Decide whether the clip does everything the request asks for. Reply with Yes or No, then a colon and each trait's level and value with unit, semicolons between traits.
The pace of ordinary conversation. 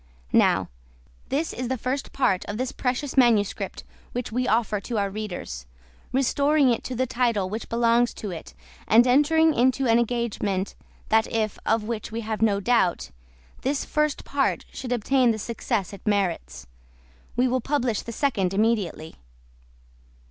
Yes: average, 155 wpm